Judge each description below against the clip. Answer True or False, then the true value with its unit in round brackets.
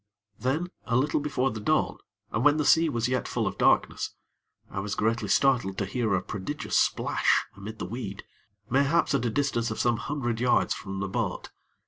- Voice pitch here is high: False (120 Hz)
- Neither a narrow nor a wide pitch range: True (4.7 semitones)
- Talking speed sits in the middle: True (190 wpm)